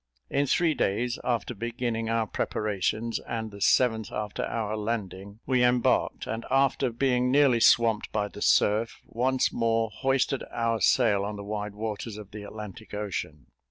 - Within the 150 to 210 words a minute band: Yes, average, 160 wpm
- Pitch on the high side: No, low, 115 Hz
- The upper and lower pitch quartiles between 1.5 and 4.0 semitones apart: Yes, average, 2.8 semitones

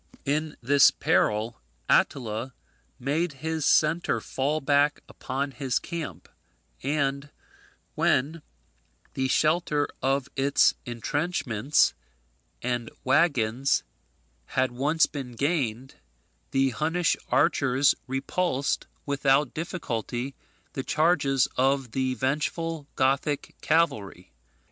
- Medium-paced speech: No, slow, 90 wpm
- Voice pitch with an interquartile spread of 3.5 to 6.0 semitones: No, average, 2.9 semitones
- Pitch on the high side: No, medium, 140 Hz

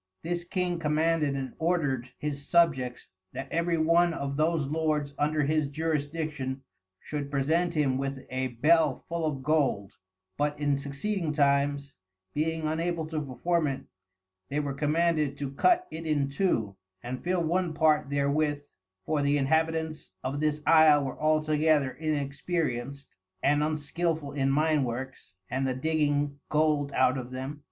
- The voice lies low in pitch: No, medium, 150 Hz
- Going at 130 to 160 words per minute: Yes, average, 145 wpm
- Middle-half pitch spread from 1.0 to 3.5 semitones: Yes, narrow, 2.5 semitones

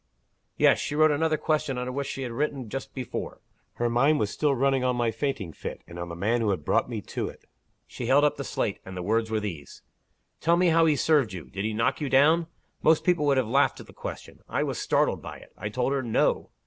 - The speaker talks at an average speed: No, fast, 250 wpm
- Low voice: Yes, low, 130 Hz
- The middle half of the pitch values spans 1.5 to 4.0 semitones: No, average, 4.9 semitones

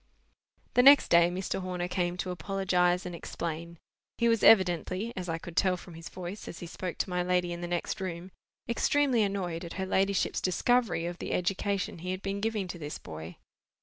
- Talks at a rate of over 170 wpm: Yes, average, 190 wpm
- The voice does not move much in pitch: Yes, narrow, 2.2 semitones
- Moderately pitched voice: Yes, medium, 180 Hz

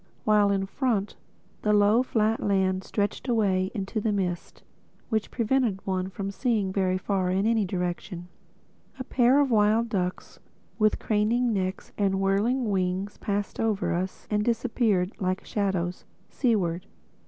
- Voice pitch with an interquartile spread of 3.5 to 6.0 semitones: No, average, 2.9 semitones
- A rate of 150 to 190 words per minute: No, average, 140 wpm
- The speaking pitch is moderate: No, high, 205 Hz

